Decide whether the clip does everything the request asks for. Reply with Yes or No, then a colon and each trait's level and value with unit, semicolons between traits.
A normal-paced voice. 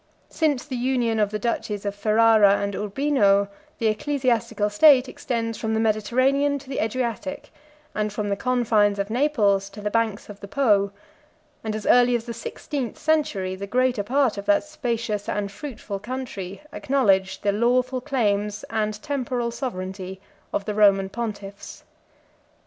Yes: average, 160 wpm